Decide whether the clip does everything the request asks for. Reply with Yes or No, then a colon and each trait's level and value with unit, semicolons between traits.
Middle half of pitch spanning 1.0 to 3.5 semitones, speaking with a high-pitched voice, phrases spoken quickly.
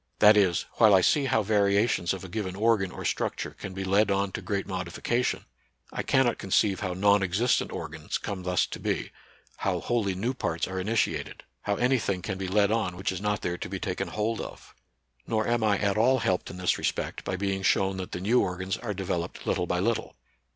No: average, 2.7 semitones; low, 100 Hz; fast, 215 wpm